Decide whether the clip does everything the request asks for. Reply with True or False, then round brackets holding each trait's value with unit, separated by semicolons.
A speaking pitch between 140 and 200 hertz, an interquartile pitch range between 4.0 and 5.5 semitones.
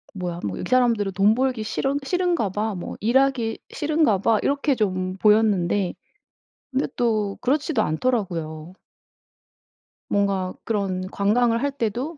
False (220 Hz; 5.1 semitones)